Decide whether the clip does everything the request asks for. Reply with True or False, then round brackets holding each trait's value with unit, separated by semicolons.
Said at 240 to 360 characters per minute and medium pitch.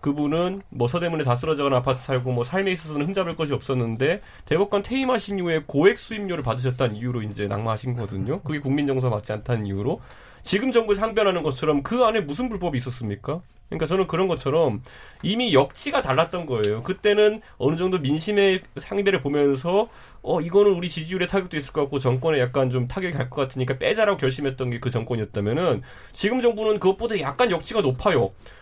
False (445 characters per minute; 150 Hz)